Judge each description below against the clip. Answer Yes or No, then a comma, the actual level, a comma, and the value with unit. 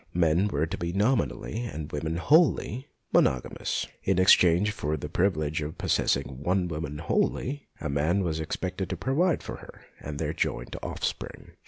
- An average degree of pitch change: Yes, average, 4.6 semitones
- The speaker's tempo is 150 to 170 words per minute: Yes, average, 155 wpm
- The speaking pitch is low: Yes, very low, 85 Hz